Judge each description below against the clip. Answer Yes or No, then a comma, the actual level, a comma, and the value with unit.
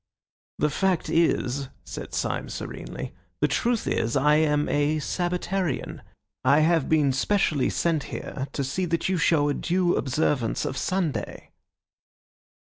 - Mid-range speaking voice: Yes, medium, 155 Hz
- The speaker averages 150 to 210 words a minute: No, slow, 135 wpm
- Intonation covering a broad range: No, average, 3.7 semitones